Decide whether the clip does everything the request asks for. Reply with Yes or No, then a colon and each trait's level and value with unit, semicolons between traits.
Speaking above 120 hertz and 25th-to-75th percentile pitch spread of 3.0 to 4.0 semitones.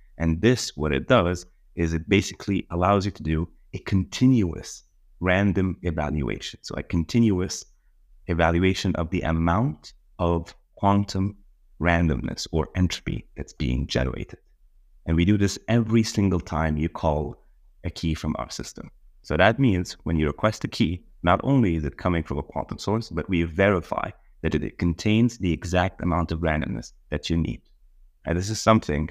No: very low, 85 Hz; average, 3.7 semitones